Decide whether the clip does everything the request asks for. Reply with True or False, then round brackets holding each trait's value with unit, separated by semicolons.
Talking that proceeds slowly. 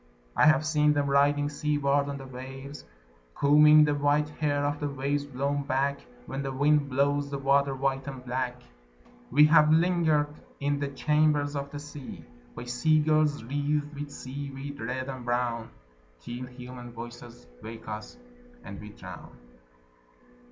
False (155 wpm)